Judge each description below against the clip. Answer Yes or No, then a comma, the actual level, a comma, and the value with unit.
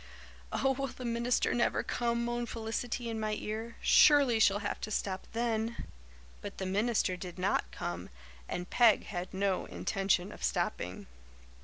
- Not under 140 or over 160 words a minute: Yes, average, 155 wpm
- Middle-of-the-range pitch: No, high, 220 Hz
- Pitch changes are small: No, average, 3.6 semitones